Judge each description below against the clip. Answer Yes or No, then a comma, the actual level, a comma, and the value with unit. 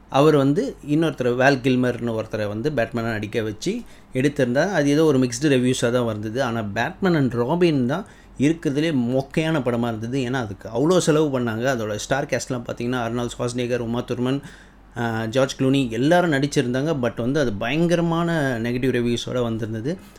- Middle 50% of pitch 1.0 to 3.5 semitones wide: No, average, 3.9 semitones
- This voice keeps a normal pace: No, fast, 150 wpm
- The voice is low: Yes, low, 130 Hz